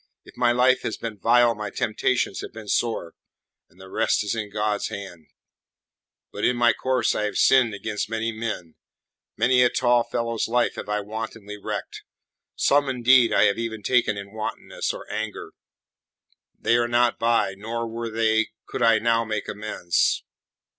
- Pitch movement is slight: Yes, narrow, 2.2 semitones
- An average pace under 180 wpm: Yes, average, 170 wpm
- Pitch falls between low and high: No, low, 115 Hz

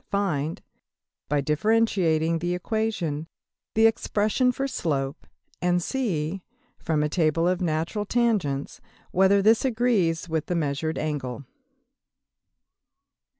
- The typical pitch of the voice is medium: Yes, medium, 175 Hz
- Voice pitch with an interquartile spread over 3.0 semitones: Yes, wide, 5.6 semitones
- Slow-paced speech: Yes, slow, 105 wpm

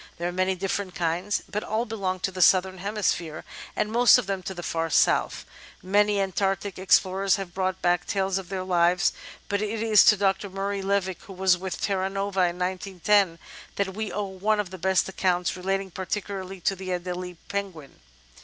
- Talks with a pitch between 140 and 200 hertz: Yes, high, 190 Hz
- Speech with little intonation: Yes, narrow, 1.6 semitones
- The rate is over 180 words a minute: Yes, average, 195 wpm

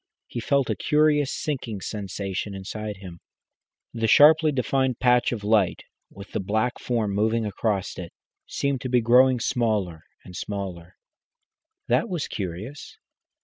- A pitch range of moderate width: Yes, average, 4.6 semitones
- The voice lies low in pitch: Yes, low, 110 Hz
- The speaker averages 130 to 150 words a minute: Yes, average, 140 wpm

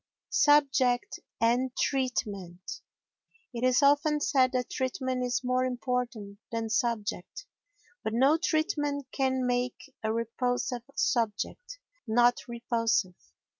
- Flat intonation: Yes, narrow, 2.3 semitones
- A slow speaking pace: Yes, slow, 105 wpm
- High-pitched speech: Yes, very high, 250 Hz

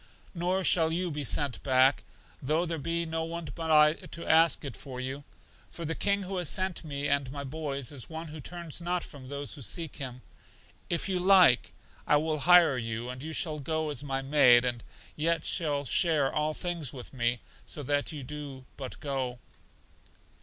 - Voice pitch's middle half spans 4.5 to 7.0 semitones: No, average, 3.7 semitones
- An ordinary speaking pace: Yes, average, 195 wpm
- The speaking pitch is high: No, medium, 150 Hz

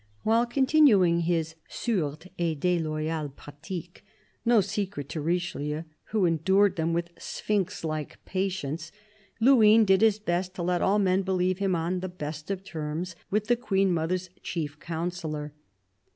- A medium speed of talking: Yes, average, 150 wpm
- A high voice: No, medium, 180 Hz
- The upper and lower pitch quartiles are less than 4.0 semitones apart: Yes, average, 3.5 semitones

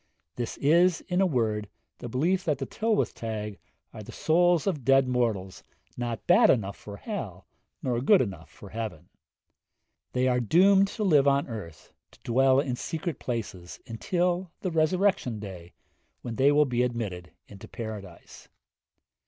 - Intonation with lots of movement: Yes, wide, 7.7 semitones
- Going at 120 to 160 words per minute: Yes, average, 155 wpm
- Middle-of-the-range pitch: No, low, 125 Hz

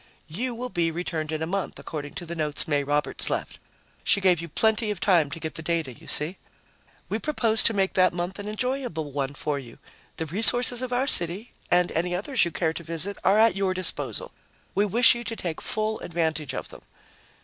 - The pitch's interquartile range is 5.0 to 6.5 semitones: Yes, average, 5.3 semitones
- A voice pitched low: No, medium, 180 Hz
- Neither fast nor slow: No, fast, 215 wpm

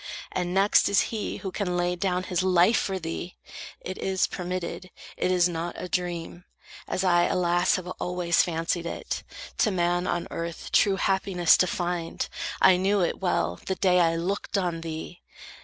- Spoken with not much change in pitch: Yes, narrow, 1.4 semitones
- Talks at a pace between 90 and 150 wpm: No, average, 175 wpm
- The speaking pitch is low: No, medium, 180 Hz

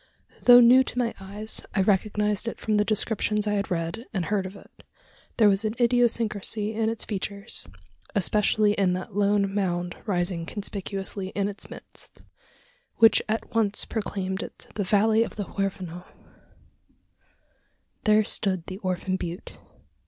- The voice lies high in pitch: Yes, high, 205 Hz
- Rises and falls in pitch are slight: Yes, narrow, 2.3 semitones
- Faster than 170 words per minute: No, average, 150 wpm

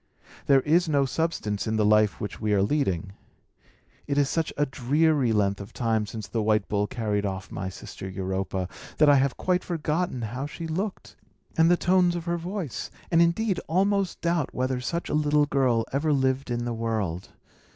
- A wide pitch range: Yes, wide, 7.3 semitones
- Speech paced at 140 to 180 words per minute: No, average, 190 wpm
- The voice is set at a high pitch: No, low, 135 Hz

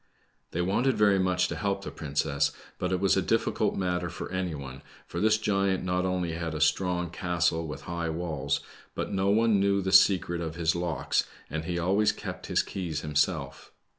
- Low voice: Yes, very low, 90 Hz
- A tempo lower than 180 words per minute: No, average, 195 wpm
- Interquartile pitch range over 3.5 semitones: No, average, 3.1 semitones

